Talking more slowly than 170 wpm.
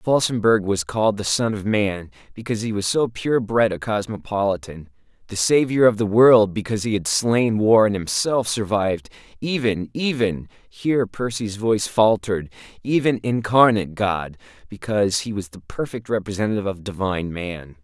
Yes: average, 140 wpm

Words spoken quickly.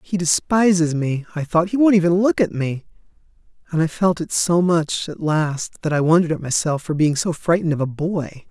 Yes: fast, 220 wpm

